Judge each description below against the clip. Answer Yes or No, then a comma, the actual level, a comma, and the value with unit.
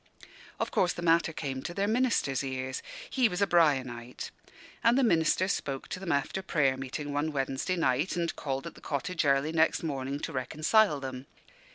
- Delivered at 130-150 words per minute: No, average, 185 wpm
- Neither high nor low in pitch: Yes, medium, 150 Hz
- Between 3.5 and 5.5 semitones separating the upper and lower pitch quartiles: Yes, average, 4.6 semitones